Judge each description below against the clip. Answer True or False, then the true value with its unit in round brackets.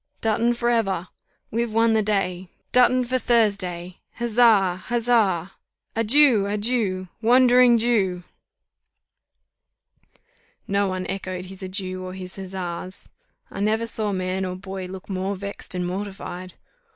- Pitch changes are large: False (3.7 semitones)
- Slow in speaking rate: True (125 wpm)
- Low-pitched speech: False (200 Hz)